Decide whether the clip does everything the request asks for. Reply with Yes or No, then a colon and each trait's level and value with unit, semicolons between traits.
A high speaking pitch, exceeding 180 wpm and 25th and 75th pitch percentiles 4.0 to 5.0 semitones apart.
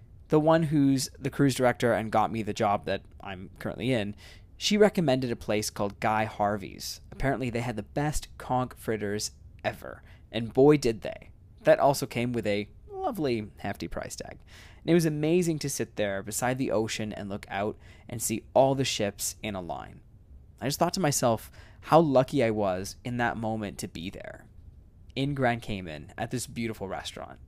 No: low, 110 Hz; average, 190 wpm; average, 4.6 semitones